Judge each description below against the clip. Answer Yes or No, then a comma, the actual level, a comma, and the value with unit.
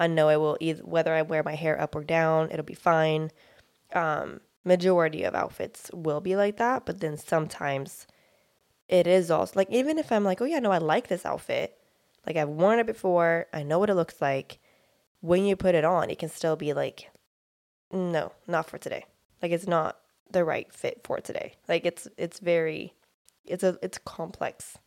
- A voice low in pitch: No, medium, 165 Hz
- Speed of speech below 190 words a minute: No, average, 200 wpm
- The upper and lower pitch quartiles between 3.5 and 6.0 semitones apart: No, average, 2.9 semitones